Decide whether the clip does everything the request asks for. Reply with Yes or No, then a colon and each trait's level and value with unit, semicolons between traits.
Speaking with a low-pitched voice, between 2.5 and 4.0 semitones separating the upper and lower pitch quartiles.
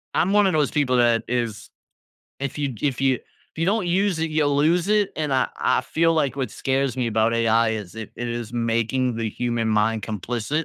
No: low, 125 Hz; average, 5.1 semitones